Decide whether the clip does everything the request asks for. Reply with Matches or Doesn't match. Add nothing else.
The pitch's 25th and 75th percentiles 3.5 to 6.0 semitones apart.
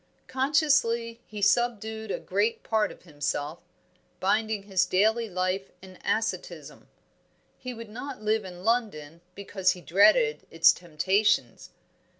Matches